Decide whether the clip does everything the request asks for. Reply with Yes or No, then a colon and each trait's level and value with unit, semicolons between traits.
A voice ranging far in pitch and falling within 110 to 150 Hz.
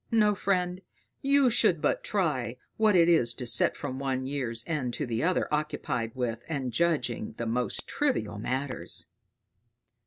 Yes: wide, 6.7 semitones; medium, 140 Hz